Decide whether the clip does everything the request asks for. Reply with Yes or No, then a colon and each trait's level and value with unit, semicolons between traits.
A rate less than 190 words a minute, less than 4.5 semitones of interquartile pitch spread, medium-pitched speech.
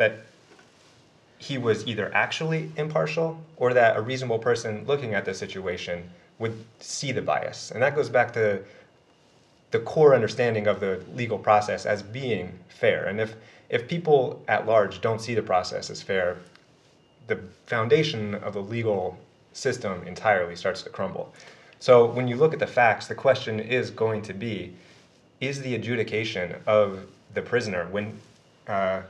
No: average, 160 wpm; average, 3.5 semitones; low, 110 Hz